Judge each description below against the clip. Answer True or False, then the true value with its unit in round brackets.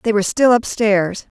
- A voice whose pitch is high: True (215 Hz)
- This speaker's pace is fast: False (175 wpm)